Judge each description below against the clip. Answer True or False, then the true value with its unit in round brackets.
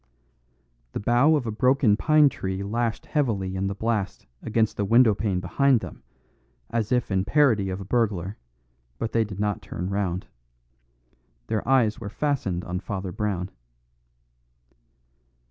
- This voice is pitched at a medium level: False (105 Hz)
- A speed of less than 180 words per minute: True (145 wpm)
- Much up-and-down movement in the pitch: False (3.8 semitones)